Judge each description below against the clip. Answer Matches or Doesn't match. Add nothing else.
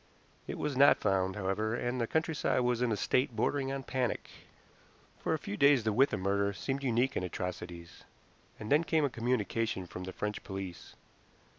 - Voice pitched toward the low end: Matches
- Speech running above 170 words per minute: Matches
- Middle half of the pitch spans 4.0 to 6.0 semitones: Matches